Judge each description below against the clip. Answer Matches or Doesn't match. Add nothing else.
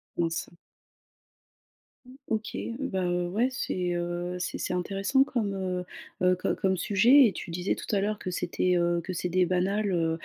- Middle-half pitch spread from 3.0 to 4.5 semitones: Doesn't match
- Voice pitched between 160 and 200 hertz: Matches